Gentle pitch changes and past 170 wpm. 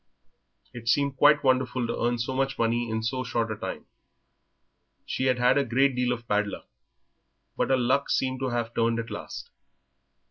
Yes: narrow, 2.1 semitones; average, 185 wpm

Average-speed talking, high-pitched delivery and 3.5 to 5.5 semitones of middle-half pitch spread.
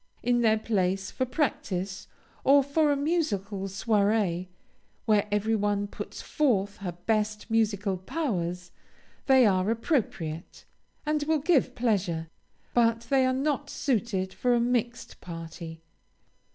No: slow, 125 wpm; high, 215 Hz; average, 5.2 semitones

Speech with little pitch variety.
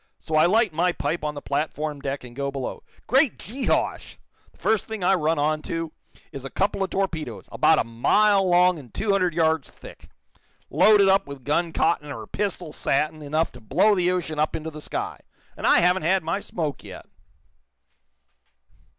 No: average, 4.3 semitones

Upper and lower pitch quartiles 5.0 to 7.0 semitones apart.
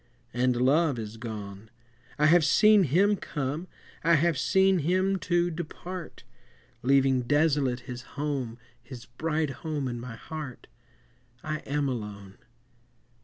Yes: average, 5.3 semitones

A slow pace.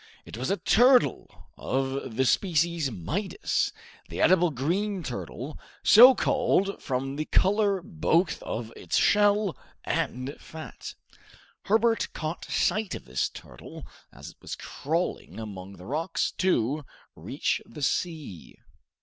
Yes: slow, 125 wpm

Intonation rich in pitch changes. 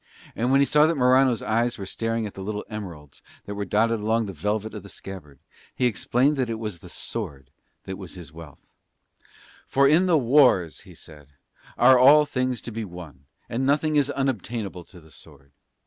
Yes: wide, 6.2 semitones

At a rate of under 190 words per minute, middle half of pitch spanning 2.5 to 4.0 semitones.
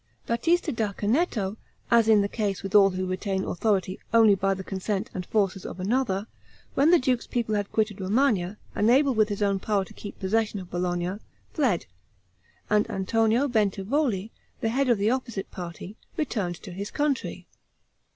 Yes: average, 170 wpm; average, 3.4 semitones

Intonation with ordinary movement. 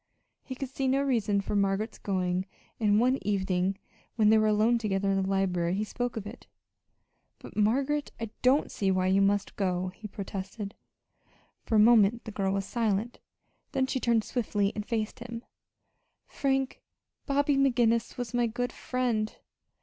Yes: average, 3.7 semitones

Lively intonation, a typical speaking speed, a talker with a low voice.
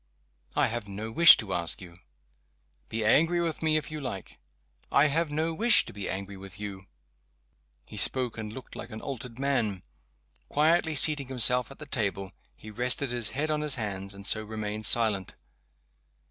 Yes: wide, 6.3 semitones; average, 175 wpm; low, 115 Hz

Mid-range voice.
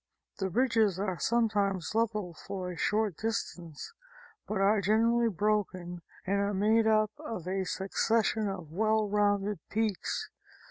No: high, 205 Hz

